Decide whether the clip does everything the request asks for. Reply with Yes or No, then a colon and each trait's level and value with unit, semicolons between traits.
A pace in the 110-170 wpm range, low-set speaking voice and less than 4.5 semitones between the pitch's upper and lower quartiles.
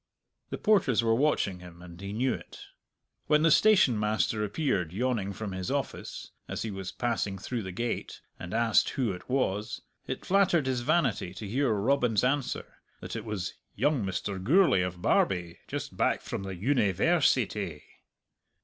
No: average, 165 wpm; low, 110 Hz; wide, 5.6 semitones